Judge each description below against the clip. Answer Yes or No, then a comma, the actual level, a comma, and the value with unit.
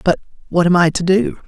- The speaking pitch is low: No, medium, 180 Hz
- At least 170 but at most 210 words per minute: Yes, fast, 205 wpm